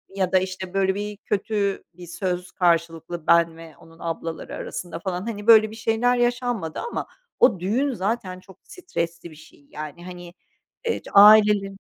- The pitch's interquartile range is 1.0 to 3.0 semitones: No, average, 4.0 semitones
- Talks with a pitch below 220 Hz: Yes, high, 190 Hz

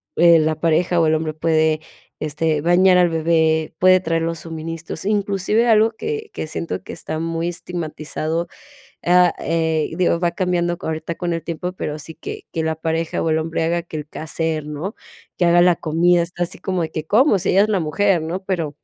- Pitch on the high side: No, medium, 165 Hz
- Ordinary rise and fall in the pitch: No, narrow, 2.0 semitones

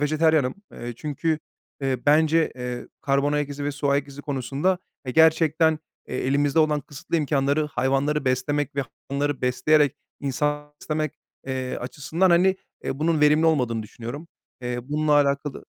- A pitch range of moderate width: No, narrow, 2.3 semitones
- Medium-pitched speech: Yes, medium, 145 Hz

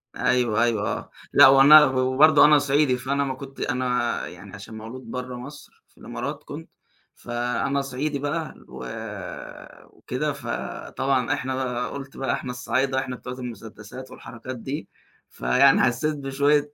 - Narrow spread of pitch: Yes, narrow, 2.2 semitones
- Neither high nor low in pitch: No, low, 130 Hz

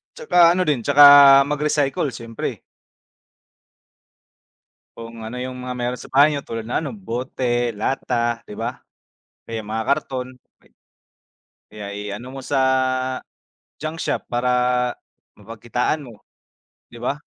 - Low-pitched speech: Yes, low, 125 Hz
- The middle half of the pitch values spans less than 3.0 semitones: No, average, 3.7 semitones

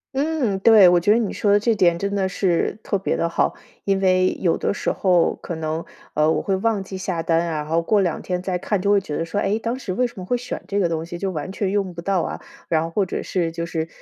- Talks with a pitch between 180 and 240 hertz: Yes, high, 190 Hz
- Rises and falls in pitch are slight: No, average, 3.3 semitones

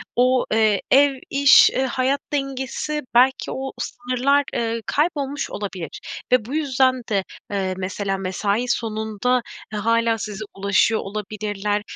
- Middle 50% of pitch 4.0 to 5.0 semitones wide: Yes, average, 4.3 semitones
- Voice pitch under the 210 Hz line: No, high, 230 Hz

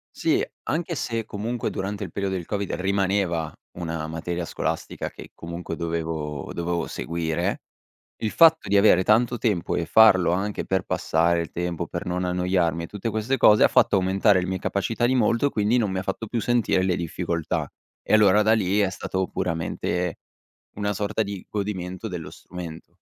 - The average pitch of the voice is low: Yes, very low, 95 Hz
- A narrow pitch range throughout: No, average, 3.5 semitones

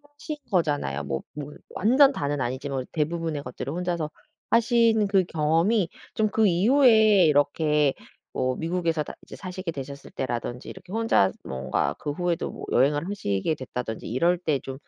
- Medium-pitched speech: Yes, medium, 160 Hz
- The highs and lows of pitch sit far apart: Yes, wide, 6.0 semitones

